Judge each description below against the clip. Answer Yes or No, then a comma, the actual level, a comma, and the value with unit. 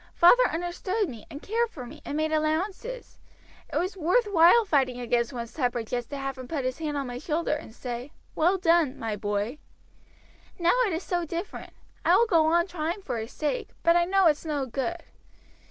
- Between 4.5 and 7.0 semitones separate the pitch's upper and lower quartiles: Yes, wide, 5.5 semitones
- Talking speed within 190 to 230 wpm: Yes, average, 200 wpm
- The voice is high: Yes, very high, 315 Hz